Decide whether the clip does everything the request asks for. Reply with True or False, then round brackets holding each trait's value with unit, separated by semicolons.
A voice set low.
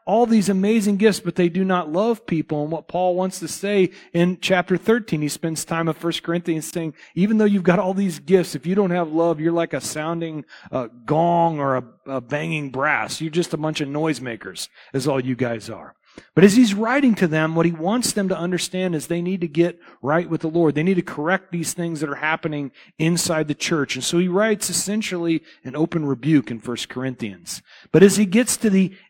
False (170 Hz)